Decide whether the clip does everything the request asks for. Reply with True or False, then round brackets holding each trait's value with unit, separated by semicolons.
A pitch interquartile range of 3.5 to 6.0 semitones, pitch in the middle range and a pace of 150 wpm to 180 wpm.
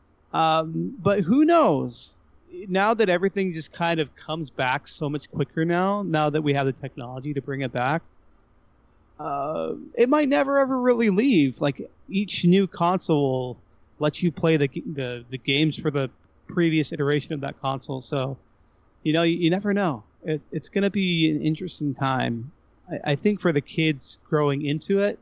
True (5.2 semitones; 155 Hz; 175 wpm)